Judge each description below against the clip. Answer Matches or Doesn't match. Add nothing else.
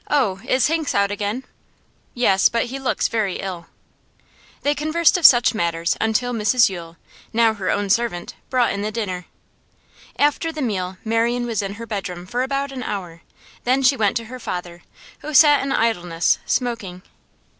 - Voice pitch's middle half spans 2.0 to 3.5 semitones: Doesn't match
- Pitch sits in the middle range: Doesn't match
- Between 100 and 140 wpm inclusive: Doesn't match